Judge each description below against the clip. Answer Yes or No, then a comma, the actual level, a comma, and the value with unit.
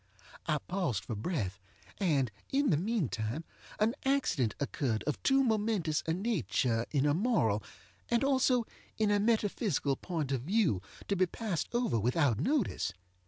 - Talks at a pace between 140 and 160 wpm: Yes, average, 150 wpm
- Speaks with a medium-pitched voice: Yes, medium, 170 Hz